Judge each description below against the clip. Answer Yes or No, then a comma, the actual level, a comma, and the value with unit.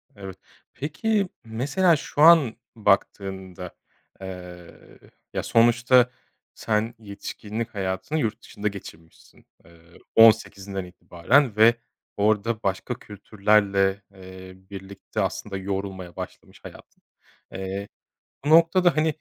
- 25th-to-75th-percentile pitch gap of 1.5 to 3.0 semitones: No, average, 3.8 semitones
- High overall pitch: No, low, 105 Hz